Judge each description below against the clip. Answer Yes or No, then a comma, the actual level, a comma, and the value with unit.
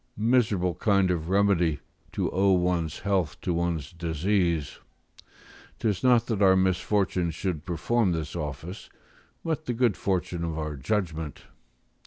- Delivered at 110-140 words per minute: Yes, slow, 135 wpm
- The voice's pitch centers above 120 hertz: No, very low, 90 Hz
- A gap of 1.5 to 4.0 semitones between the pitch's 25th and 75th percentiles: Yes, average, 3.6 semitones